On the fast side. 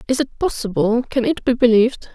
No: average, 195 wpm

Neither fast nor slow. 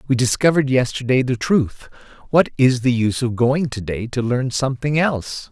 Yes: average, 185 wpm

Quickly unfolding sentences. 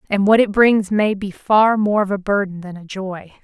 Yes: fast, 245 wpm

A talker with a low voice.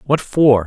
Yes: low, 130 Hz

